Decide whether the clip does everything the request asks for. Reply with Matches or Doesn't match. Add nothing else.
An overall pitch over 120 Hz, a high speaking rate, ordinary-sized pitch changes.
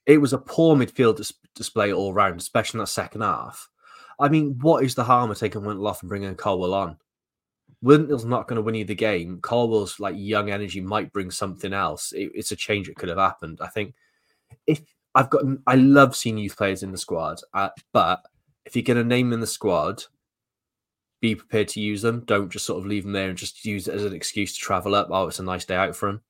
Doesn't match